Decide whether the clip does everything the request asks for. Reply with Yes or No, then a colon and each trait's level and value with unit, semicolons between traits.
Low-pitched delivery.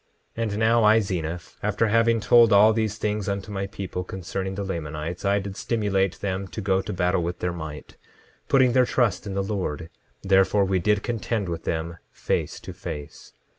Yes: low, 100 Hz